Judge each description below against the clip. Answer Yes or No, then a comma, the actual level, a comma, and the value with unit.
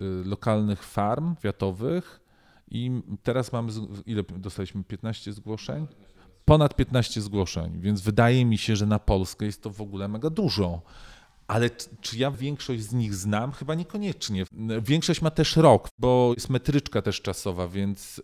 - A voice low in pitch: Yes, low, 110 Hz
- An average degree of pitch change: Yes, average, 4.3 semitones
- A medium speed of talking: Yes, average, 150 wpm